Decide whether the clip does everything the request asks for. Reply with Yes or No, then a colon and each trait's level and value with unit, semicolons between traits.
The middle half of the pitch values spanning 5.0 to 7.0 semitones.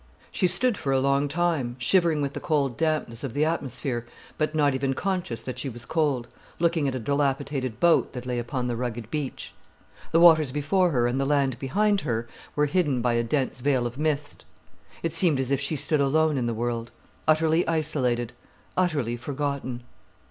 No: average, 4.1 semitones